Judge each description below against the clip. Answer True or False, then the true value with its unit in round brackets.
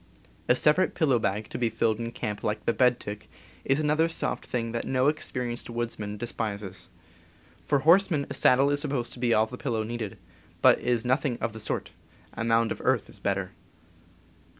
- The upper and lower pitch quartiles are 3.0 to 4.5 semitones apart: True (3.8 semitones)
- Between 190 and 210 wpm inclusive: True (200 wpm)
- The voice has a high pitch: False (120 Hz)